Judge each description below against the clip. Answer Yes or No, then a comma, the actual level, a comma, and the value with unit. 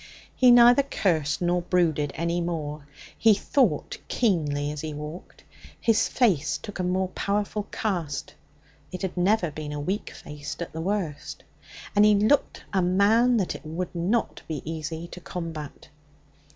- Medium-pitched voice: Yes, medium, 175 Hz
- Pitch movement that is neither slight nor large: Yes, average, 4.9 semitones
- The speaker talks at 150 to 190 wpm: Yes, average, 155 wpm